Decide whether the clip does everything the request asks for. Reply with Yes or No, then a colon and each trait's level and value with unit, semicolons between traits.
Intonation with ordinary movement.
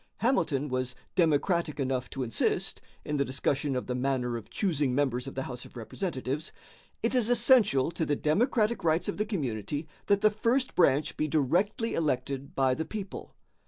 No: wide, 6.8 semitones